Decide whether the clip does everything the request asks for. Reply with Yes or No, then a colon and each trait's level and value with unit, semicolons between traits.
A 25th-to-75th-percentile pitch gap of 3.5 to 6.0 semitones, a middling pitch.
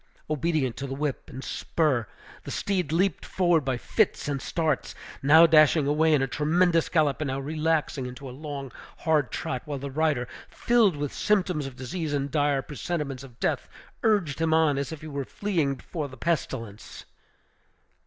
No: average, 3.1 semitones; medium, 150 Hz